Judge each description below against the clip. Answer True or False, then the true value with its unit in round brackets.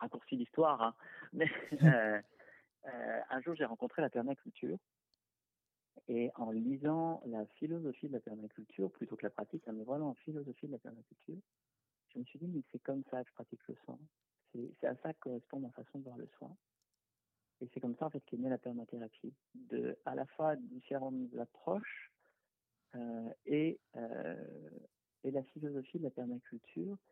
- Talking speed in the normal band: True (175 wpm)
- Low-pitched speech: True (130 Hz)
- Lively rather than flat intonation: False (4.5 semitones)